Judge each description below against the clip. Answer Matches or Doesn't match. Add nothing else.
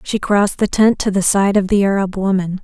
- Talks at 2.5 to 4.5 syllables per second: Doesn't match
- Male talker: Doesn't match